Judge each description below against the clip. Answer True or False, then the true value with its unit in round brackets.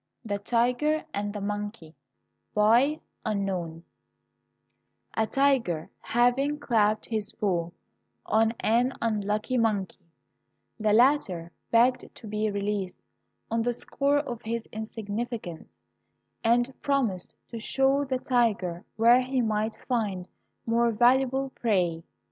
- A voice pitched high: True (225 Hz)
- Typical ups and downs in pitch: True (3.4 semitones)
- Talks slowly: True (110 wpm)